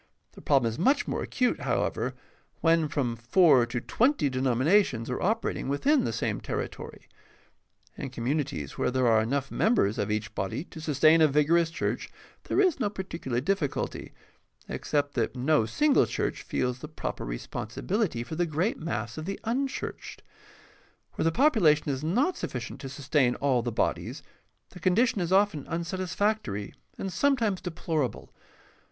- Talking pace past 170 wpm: No, average, 160 wpm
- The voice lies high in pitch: No, medium, 155 Hz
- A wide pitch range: Yes, wide, 7.2 semitones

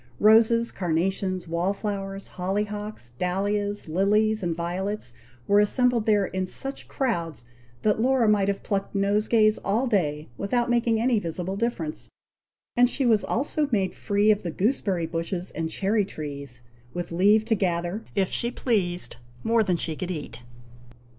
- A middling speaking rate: Yes, average, 155 wpm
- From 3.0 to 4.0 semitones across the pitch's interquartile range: Yes, average, 3.7 semitones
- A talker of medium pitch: No, high, 200 Hz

